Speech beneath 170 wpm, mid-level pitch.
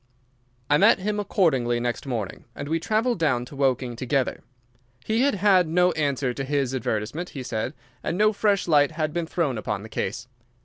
No: average, 185 wpm; medium, 145 Hz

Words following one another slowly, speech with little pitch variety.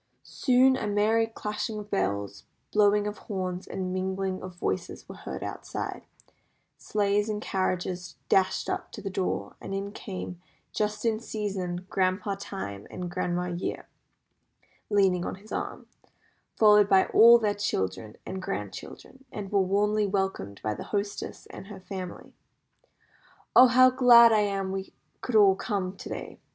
No: average, 150 wpm; narrow, 2.2 semitones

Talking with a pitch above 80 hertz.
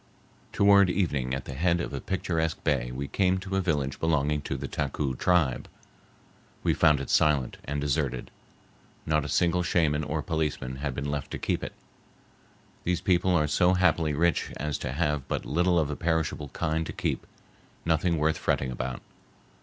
No: very low, 75 Hz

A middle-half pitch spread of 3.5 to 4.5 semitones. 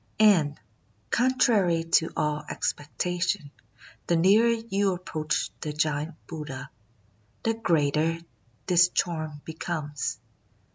Yes: average, 3.8 semitones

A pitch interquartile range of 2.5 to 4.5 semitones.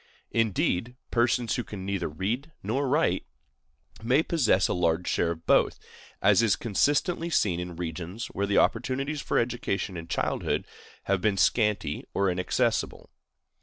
No: wide, 5.4 semitones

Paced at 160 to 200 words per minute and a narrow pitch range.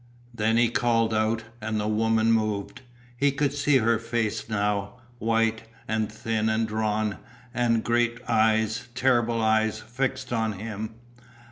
No: average, 140 wpm; narrow, 1.3 semitones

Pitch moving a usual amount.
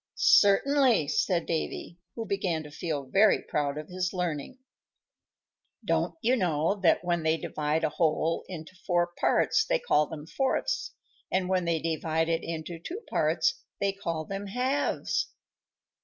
Yes: average, 4.0 semitones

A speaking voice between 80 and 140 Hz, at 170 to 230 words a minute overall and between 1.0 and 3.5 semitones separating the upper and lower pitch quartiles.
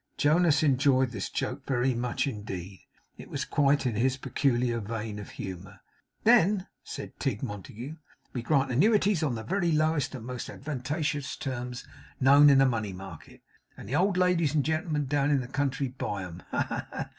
No: low, 135 Hz; average, 180 wpm; average, 4.5 semitones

